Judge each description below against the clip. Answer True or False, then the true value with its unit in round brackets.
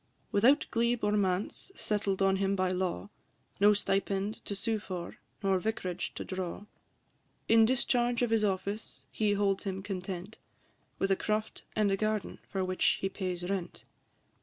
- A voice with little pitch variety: True (2.2 semitones)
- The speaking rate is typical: True (160 wpm)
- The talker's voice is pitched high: True (200 Hz)